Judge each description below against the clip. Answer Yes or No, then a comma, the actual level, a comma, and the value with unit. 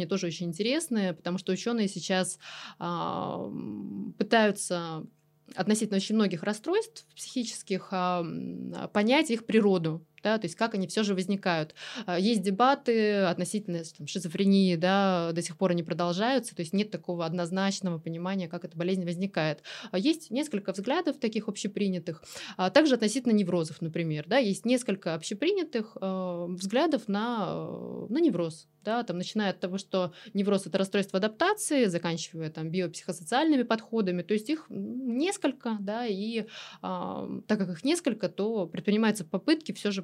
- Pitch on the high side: Yes, high, 195 Hz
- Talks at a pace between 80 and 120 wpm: No, average, 140 wpm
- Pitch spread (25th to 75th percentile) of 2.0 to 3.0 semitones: No, average, 4.1 semitones